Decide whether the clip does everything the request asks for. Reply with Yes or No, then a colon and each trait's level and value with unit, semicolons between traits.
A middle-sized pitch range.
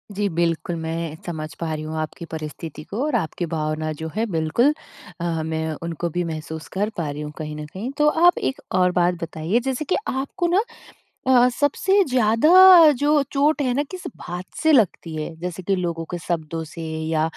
No: wide, 8.5 semitones